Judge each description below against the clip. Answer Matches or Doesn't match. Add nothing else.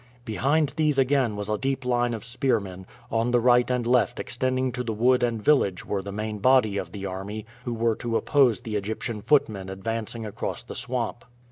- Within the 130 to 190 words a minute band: Doesn't match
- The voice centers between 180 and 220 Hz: Doesn't match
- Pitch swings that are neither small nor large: Matches